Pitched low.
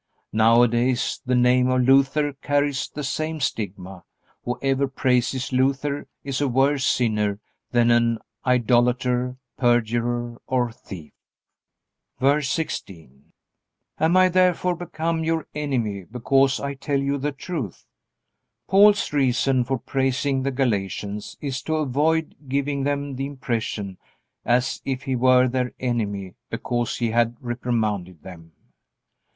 Yes: low, 130 Hz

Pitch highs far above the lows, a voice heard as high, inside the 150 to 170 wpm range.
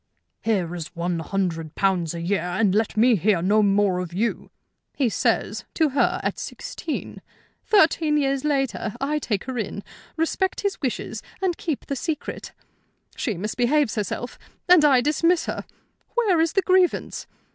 Yes: wide, 7.8 semitones; high, 240 Hz; average, 155 wpm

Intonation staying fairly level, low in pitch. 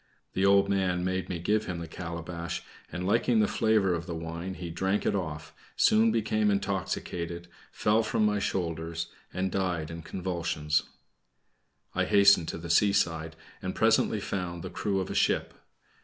No: average, 3.0 semitones; very low, 90 Hz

